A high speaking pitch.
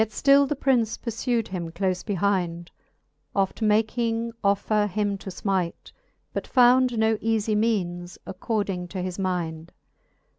Yes: high, 205 Hz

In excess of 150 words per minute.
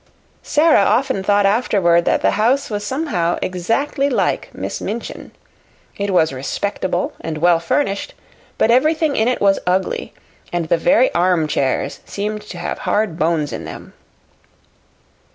No: average, 140 wpm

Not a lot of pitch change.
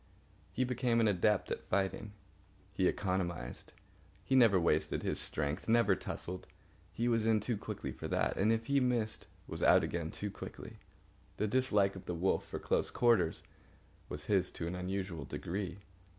No: average, 4.2 semitones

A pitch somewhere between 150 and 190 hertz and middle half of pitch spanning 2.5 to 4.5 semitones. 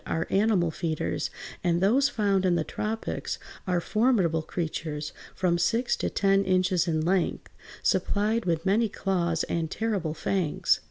Yes: medium, 185 Hz; average, 3.6 semitones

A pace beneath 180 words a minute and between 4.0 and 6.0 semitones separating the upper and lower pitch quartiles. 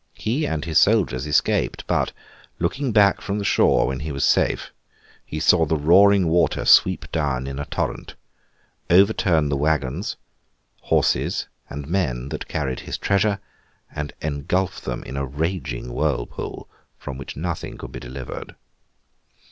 Yes: average, 150 wpm; average, 5.3 semitones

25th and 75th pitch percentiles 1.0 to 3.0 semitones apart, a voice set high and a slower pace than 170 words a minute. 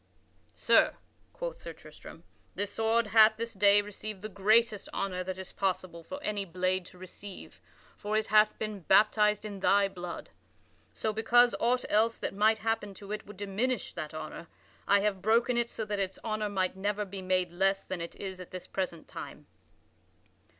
No: narrow, 2.5 semitones; high, 205 Hz; average, 180 wpm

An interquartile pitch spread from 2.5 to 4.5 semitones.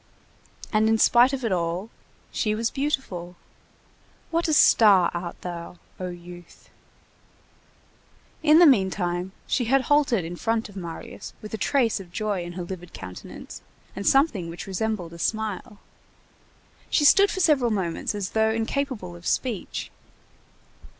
No: wide, 5.5 semitones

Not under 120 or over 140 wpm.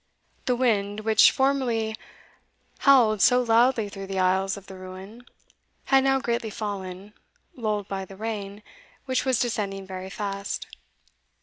Yes: slow, 135 wpm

